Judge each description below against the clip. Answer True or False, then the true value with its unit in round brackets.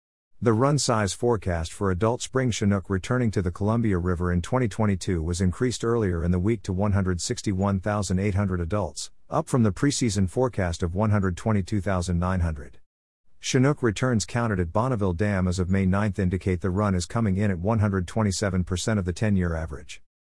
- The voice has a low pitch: True (100 Hz)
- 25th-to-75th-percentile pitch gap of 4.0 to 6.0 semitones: False (3.6 semitones)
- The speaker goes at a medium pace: True (160 wpm)